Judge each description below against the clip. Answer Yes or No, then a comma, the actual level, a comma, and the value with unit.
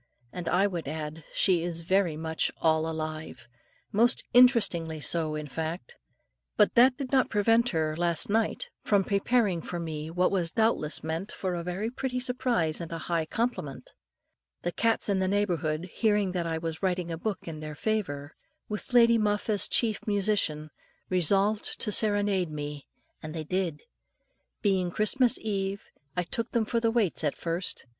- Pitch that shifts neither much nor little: Yes, average, 4.9 semitones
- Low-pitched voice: No, medium, 180 Hz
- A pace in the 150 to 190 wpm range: Yes, average, 170 wpm